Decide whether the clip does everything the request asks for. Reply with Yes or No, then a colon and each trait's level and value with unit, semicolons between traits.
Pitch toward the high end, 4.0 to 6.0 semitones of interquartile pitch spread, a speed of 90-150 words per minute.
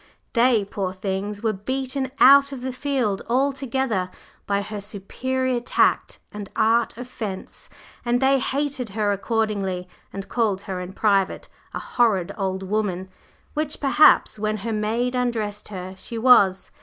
Yes: high, 220 Hz; average, 4.5 semitones; average, 145 wpm